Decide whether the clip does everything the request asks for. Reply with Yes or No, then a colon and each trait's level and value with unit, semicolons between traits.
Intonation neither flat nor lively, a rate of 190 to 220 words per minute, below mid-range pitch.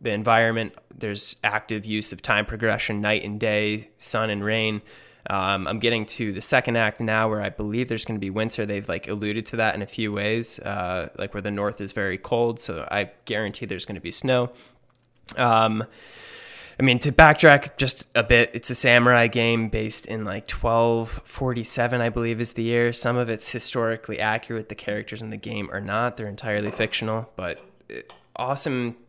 No: narrow, 2.1 semitones; average, 195 wpm; low, 110 Hz